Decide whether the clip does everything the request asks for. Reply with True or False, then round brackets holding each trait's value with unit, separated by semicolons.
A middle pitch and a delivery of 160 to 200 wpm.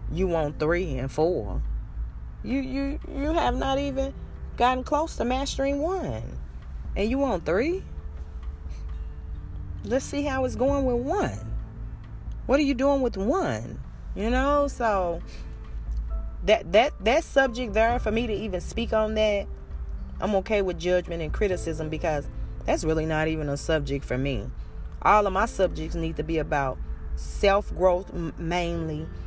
False (170 Hz; 150 wpm)